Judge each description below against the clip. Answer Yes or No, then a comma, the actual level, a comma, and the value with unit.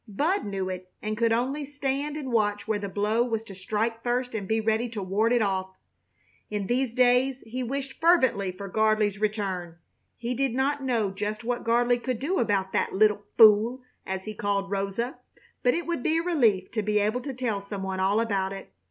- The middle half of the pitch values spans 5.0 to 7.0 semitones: No, average, 3.8 semitones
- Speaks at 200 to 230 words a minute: Yes, fast, 205 wpm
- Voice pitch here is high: Yes, high, 220 Hz